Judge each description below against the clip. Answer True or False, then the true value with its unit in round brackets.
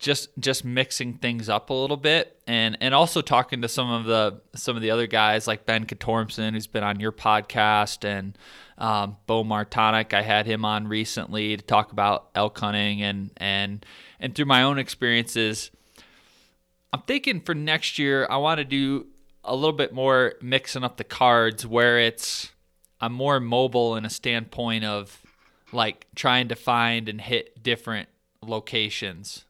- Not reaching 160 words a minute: False (170 wpm)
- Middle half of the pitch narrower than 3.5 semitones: True (3.1 semitones)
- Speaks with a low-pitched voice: True (115 Hz)